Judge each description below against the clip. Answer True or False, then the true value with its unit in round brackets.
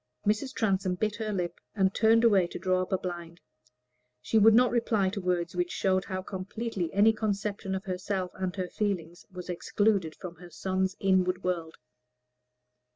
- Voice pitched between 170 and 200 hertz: True (190 Hz)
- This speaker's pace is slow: False (170 wpm)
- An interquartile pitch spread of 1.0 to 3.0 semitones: True (2.4 semitones)